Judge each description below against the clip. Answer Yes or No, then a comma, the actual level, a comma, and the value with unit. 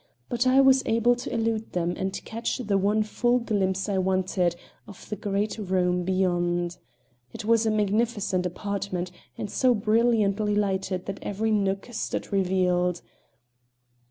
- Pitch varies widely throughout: No, average, 3.1 semitones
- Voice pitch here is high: Yes, high, 200 Hz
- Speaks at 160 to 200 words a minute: No, average, 145 wpm